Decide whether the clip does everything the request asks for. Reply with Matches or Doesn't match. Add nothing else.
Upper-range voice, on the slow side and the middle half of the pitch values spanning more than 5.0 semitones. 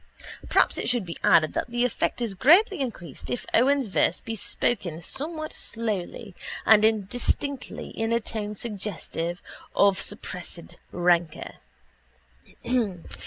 Matches